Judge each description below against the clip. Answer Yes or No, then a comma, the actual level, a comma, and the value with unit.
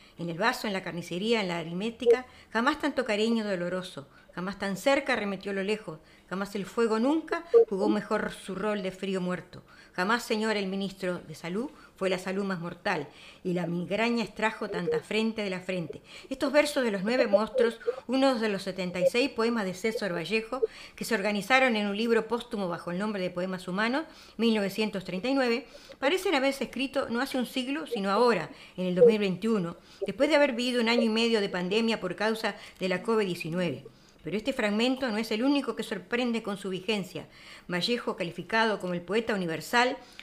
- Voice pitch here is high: Yes, high, 215 Hz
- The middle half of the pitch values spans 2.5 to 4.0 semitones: No, average, 4.6 semitones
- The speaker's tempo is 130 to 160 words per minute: No, average, 185 wpm